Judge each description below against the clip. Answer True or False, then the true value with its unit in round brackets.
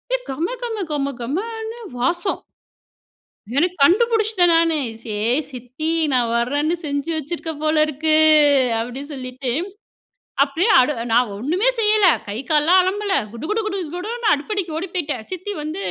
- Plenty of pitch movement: True (6.1 semitones)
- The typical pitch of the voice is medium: False (325 Hz)